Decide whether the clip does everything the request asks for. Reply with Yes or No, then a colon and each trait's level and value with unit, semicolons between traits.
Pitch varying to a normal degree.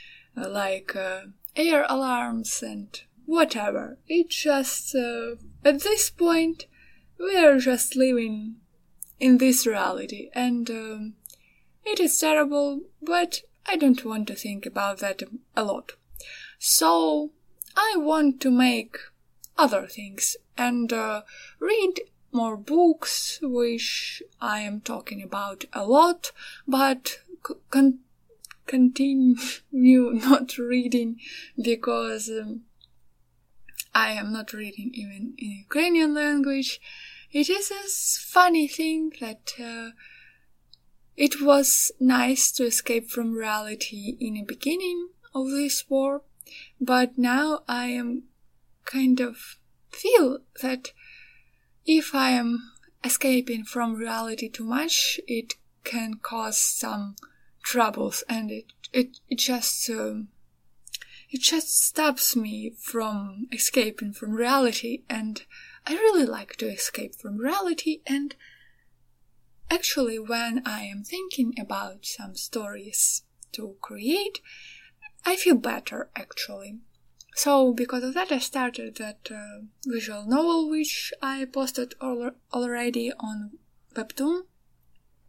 Yes: average, 4.7 semitones